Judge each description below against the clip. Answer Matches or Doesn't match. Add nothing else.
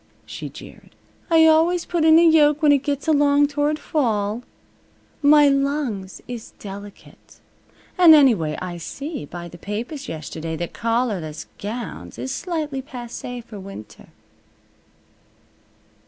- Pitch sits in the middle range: Doesn't match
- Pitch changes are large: Matches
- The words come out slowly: Matches